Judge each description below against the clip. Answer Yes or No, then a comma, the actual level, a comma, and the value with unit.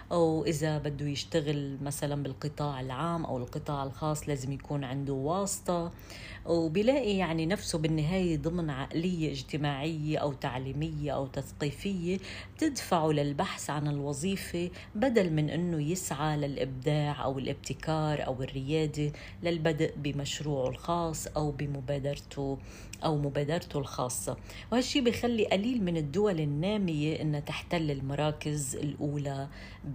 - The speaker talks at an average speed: Yes, average, 110 wpm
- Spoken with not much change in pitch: No, average, 3.0 semitones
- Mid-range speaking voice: Yes, medium, 150 Hz